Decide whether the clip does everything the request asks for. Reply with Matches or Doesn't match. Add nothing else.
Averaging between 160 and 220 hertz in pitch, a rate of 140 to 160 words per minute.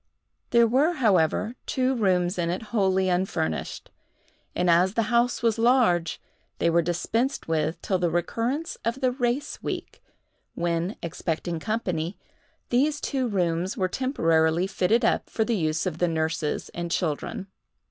Matches